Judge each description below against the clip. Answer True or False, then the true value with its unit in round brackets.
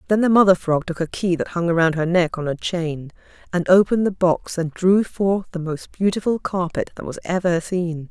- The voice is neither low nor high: True (175 Hz)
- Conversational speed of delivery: False (220 wpm)